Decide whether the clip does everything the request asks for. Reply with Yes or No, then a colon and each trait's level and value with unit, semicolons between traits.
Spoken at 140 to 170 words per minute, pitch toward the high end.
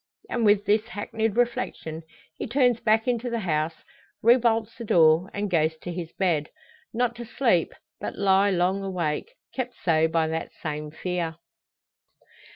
Yes: average, 155 wpm; high, 195 Hz